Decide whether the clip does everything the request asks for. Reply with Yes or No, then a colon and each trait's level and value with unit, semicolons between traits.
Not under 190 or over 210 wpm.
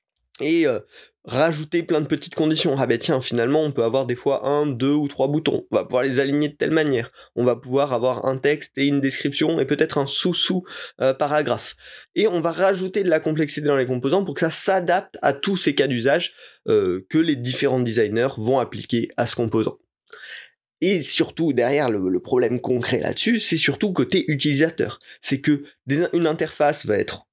Yes: average, 200 wpm